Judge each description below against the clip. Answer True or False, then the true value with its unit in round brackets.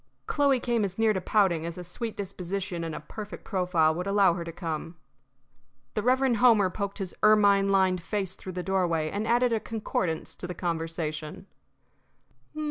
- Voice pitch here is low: False (190 Hz)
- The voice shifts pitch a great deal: False (3.8 semitones)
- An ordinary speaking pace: True (175 wpm)